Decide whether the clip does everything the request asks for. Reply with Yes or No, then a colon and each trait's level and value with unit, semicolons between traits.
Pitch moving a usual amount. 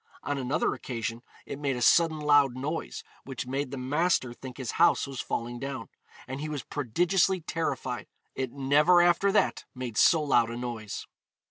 Yes: average, 3.7 semitones